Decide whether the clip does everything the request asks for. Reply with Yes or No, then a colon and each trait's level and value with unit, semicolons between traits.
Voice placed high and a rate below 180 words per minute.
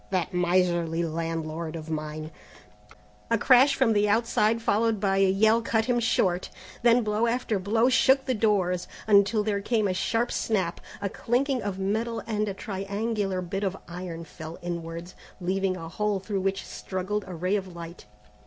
Yes: high, 195 Hz; average, 170 wpm